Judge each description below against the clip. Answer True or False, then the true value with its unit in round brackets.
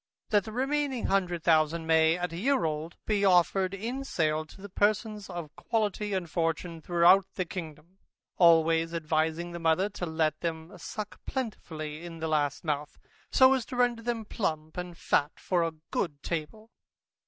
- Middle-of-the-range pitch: True (175 Hz)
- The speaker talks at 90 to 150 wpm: False (170 wpm)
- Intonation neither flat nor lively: True (4.4 semitones)